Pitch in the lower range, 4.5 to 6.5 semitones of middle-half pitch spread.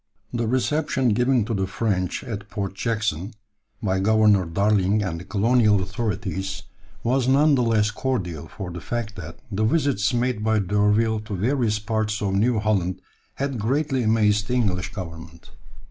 No: low, 105 Hz; average, 3.5 semitones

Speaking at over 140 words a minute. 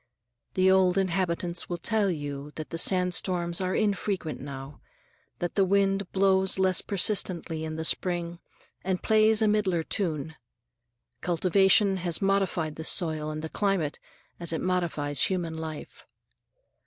No: slow, 135 wpm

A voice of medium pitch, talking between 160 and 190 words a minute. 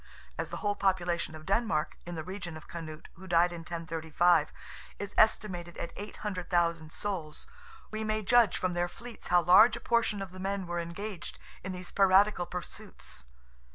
Yes: medium, 180 Hz; average, 170 wpm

